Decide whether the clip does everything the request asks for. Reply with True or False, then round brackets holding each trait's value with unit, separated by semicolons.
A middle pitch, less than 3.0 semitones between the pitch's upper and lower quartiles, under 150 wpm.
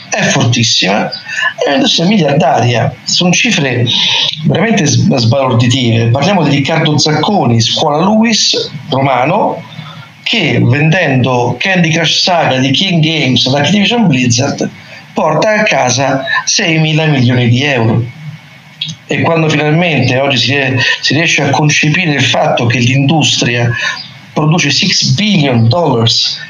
False (150 Hz; 4.5 semitones; 120 wpm)